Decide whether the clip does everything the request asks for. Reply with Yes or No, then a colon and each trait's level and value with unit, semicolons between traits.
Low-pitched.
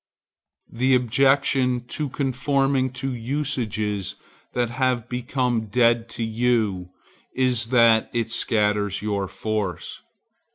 Yes: low, 120 Hz